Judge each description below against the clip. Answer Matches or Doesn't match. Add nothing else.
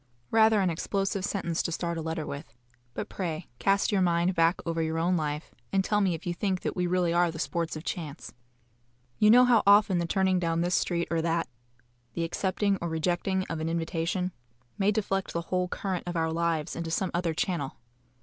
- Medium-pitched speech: Matches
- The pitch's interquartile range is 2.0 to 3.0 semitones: Matches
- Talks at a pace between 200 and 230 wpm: Matches